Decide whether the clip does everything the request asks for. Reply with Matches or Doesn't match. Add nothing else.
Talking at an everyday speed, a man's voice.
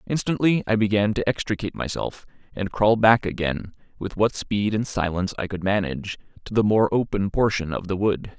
Matches